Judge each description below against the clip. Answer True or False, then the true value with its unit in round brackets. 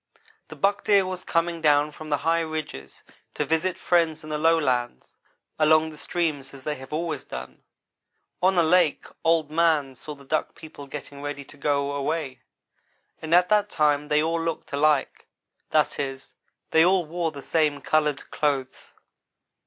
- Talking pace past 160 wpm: True (170 wpm)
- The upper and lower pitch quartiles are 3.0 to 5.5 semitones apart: False (2.6 semitones)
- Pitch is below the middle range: False (155 Hz)